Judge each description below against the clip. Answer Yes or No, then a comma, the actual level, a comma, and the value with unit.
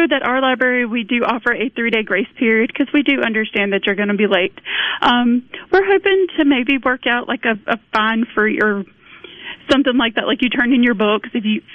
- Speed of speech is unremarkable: No, fast, 225 wpm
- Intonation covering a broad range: No, average, 3.6 semitones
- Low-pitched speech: No, high, 240 Hz